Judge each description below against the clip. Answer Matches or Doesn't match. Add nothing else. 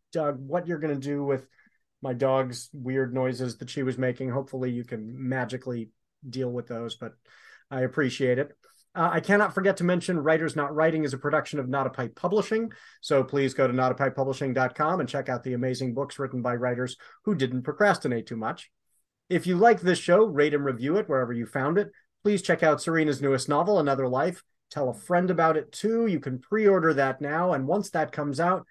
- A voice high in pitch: Doesn't match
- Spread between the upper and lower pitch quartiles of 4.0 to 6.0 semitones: Matches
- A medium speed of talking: Doesn't match